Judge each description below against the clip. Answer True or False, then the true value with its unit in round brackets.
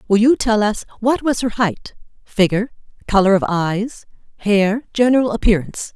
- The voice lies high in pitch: True (215 Hz)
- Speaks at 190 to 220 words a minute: False (150 wpm)